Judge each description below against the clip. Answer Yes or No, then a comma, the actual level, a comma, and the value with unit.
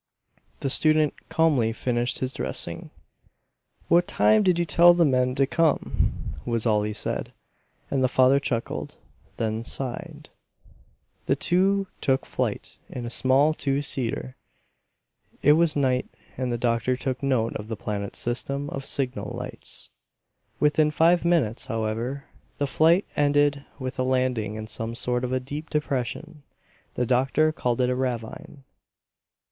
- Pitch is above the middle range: No, low, 130 Hz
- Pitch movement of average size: Yes, average, 3.8 semitones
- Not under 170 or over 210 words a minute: No, average, 145 wpm